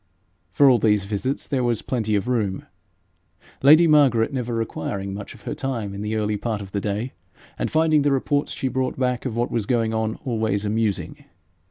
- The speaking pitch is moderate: No, low, 115 Hz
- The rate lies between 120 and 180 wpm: No, average, 190 wpm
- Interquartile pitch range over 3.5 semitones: Yes, average, 3.9 semitones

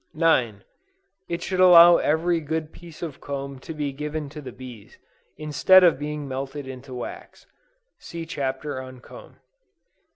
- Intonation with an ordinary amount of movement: Yes, average, 3.7 semitones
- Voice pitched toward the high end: No, medium, 150 Hz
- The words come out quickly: No, average, 150 wpm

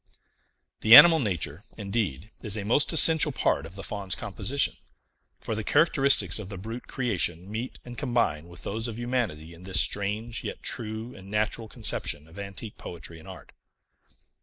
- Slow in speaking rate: No, average, 165 wpm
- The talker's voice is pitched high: No, low, 105 Hz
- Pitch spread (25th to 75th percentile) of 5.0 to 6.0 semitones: No, average, 4.2 semitones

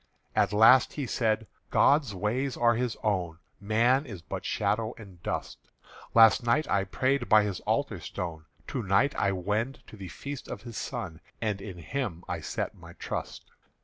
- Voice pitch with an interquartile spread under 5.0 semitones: Yes, average, 4.2 semitones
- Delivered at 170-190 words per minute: Yes, average, 175 wpm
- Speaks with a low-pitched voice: Yes, low, 110 Hz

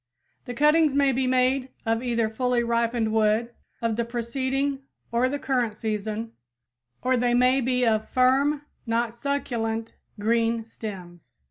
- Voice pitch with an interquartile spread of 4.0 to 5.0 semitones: No, narrow, 2.5 semitones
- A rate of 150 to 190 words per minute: No, average, 140 wpm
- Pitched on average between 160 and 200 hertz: No, high, 235 Hz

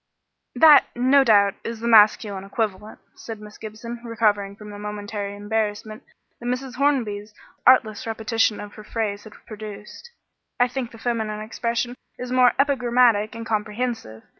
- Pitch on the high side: Yes, high, 220 Hz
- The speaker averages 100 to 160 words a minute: Yes, average, 145 wpm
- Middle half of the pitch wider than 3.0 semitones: No, narrow, 2.6 semitones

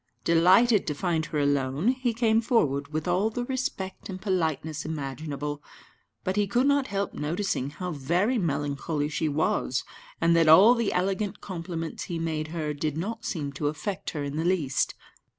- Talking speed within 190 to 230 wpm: No, average, 170 wpm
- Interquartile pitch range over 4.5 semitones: Yes, average, 5.1 semitones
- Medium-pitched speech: Yes, medium, 165 Hz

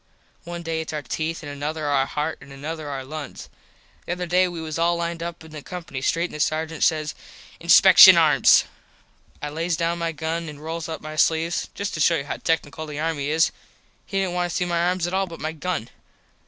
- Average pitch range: No, narrow, 2.0 semitones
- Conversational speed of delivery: No, fast, 225 wpm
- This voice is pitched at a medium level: Yes, medium, 160 Hz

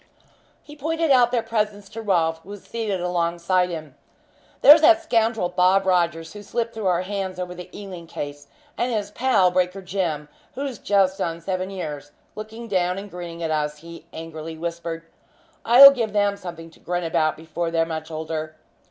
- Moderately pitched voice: Yes, medium, 180 Hz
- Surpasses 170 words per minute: Yes, average, 180 wpm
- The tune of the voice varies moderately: Yes, average, 4.2 semitones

